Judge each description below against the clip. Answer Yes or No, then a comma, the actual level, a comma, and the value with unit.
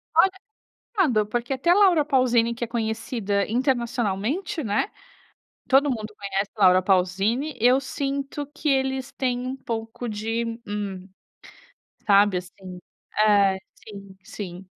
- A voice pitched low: No, high, 230 Hz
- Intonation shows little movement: No, average, 4.8 semitones